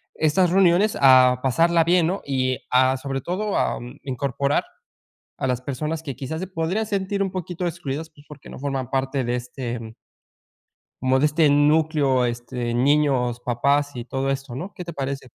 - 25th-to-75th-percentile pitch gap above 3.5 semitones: Yes, average, 4.1 semitones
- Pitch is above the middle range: No, medium, 140 Hz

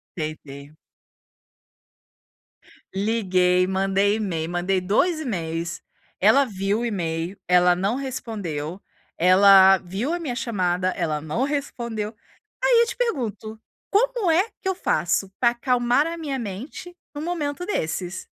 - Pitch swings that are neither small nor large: No, wide, 7.3 semitones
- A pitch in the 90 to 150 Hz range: No, high, 205 Hz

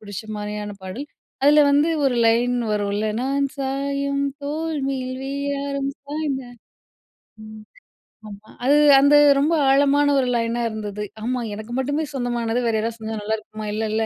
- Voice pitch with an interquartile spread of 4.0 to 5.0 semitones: Yes, average, 4.4 semitones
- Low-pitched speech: No, very high, 255 Hz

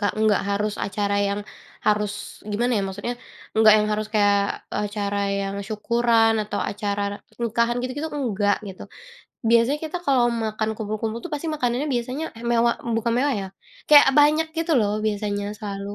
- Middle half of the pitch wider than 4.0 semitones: No, average, 3.0 semitones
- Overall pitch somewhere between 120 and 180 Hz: No, high, 220 Hz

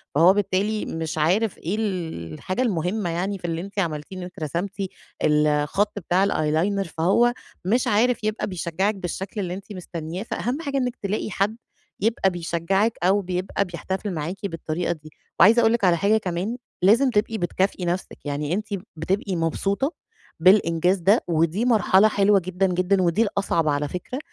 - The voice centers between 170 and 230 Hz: Yes, high, 190 Hz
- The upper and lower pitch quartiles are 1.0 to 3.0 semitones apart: No, average, 3.6 semitones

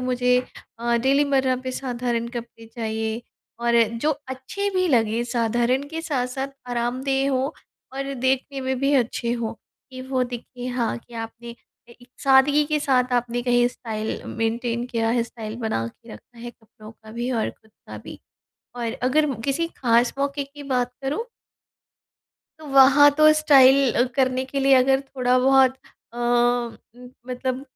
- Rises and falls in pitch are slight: Yes, narrow, 2.3 semitones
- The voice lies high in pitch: Yes, very high, 250 Hz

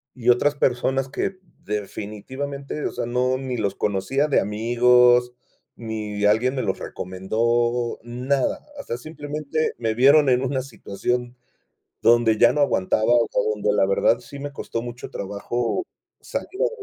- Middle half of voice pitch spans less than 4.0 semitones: Yes, average, 3.5 semitones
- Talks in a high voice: No, low, 120 Hz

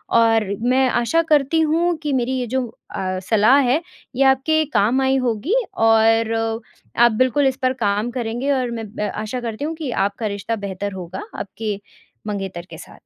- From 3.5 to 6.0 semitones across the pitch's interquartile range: Yes, average, 3.8 semitones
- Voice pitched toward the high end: Yes, high, 240 Hz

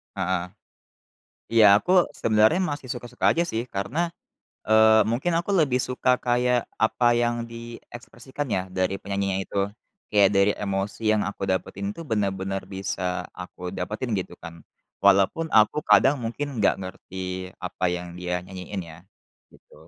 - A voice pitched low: Yes, low, 105 Hz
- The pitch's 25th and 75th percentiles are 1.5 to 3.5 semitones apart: No, average, 4.1 semitones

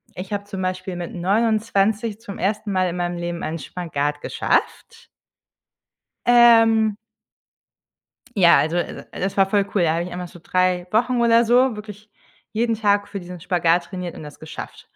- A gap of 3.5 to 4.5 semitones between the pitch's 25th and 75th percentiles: Yes, average, 3.8 semitones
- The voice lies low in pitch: No, high, 195 Hz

